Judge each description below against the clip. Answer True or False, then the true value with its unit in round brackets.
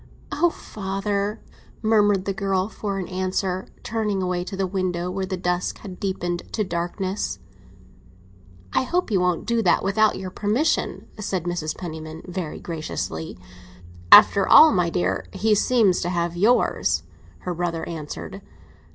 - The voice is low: False (190 Hz)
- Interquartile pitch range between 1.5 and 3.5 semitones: True (2.7 semitones)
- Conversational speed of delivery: True (145 wpm)